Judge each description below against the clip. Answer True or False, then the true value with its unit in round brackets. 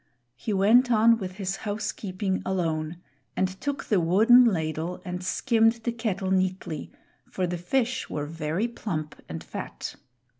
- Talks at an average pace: True (145 wpm)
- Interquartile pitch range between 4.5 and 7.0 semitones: True (4.8 semitones)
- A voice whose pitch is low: False (190 Hz)